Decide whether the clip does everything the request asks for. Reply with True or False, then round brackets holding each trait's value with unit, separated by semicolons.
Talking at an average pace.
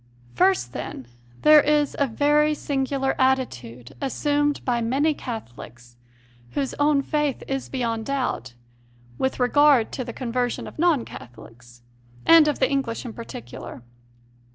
False (130 wpm)